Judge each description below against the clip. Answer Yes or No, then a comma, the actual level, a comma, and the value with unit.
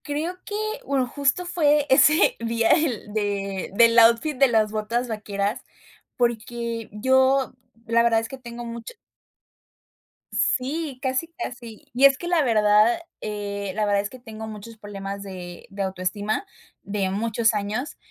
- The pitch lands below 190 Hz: No, high, 230 Hz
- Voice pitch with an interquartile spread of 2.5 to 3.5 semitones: No, average, 4.0 semitones